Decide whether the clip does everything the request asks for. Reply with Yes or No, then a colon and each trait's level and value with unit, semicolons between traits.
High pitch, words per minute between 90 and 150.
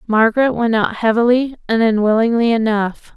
Yes: high, 225 Hz; slow, 135 wpm